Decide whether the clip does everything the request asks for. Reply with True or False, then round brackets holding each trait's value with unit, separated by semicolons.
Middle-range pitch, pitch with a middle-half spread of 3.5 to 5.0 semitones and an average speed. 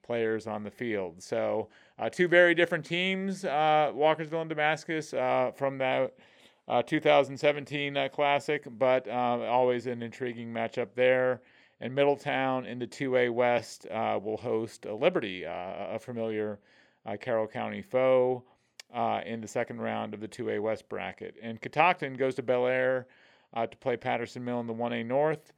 False (125 Hz; 3.9 semitones; 165 wpm)